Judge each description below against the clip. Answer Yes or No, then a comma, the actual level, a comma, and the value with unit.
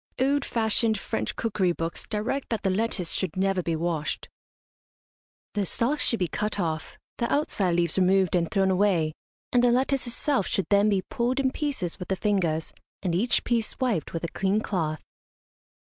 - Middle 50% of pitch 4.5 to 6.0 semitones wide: Yes, average, 5.1 semitones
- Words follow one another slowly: No, average, 175 wpm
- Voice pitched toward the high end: Yes, high, 195 Hz